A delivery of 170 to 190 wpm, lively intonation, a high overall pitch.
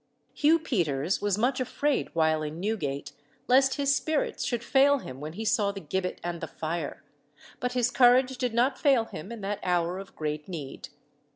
Yes: average, 185 wpm; wide, 7.5 semitones; high, 210 Hz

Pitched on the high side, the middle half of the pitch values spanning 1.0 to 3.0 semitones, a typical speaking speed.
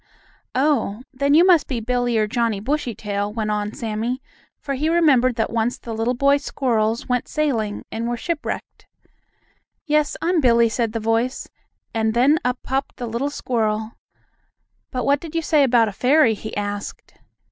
No: high, 240 Hz; average, 4.1 semitones; average, 170 wpm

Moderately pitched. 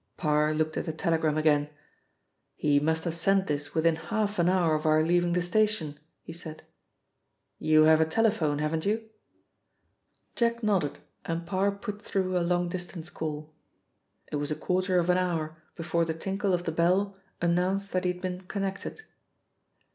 Yes: medium, 170 Hz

